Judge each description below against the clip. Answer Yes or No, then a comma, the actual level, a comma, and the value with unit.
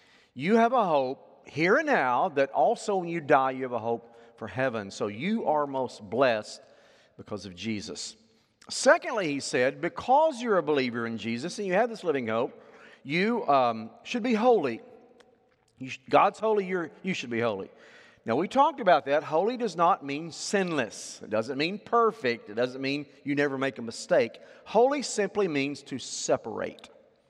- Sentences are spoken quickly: No, average, 180 wpm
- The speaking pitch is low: No, medium, 160 Hz